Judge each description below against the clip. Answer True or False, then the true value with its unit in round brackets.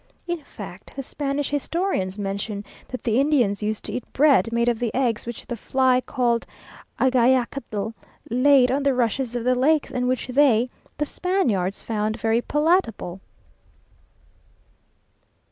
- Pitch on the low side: False (250 Hz)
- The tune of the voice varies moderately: True (3.7 semitones)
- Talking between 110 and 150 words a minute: True (145 wpm)